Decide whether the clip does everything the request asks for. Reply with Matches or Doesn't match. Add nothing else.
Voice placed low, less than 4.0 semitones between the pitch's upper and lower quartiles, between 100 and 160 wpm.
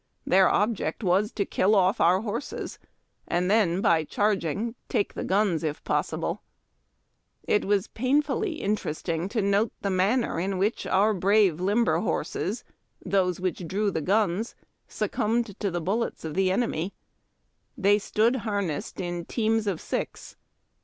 Doesn't match